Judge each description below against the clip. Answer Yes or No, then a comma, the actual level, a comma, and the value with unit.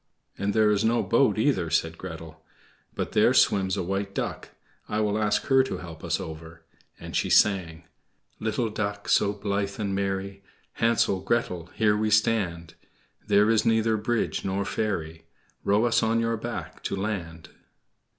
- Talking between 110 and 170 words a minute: Yes, average, 160 wpm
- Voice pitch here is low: Yes, low, 100 Hz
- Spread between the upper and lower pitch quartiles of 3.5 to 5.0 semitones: No, average, 3.0 semitones